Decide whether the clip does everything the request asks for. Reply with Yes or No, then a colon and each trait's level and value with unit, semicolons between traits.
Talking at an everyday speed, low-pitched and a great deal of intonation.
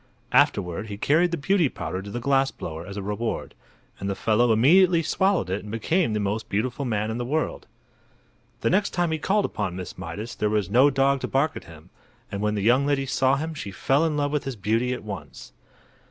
No: fast, 225 wpm; low, 120 Hz; wide, 5.9 semitones